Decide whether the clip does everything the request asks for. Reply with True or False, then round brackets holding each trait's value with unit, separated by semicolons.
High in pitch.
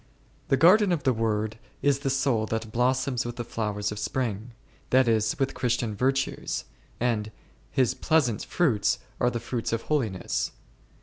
False (120 Hz)